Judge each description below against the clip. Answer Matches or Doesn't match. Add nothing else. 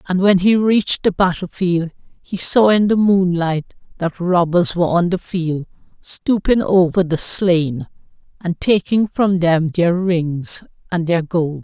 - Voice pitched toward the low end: Doesn't match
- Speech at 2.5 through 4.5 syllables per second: Matches